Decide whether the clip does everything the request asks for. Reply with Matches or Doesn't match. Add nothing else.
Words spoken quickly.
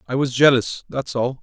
Matches